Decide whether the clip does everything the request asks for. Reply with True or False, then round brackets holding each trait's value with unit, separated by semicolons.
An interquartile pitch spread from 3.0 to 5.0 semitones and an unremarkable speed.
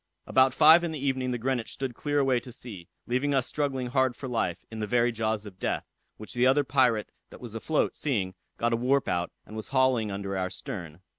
False (3.5 semitones; 225 wpm)